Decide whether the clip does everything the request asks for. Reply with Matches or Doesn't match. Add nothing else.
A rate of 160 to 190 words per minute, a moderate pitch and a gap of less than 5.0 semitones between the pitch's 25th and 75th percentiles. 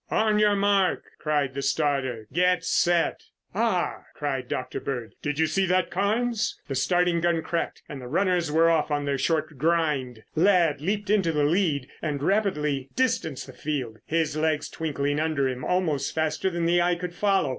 Matches